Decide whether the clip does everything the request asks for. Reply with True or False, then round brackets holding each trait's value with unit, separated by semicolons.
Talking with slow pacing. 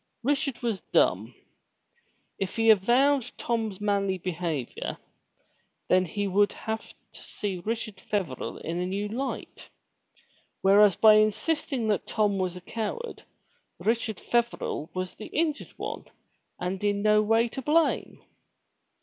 True (130 wpm)